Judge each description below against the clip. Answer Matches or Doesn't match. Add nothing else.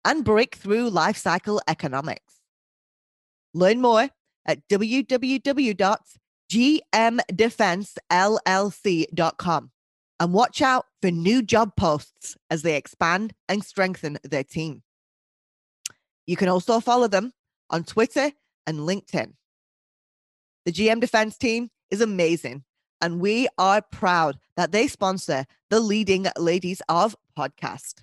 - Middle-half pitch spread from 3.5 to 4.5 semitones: Doesn't match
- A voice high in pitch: Matches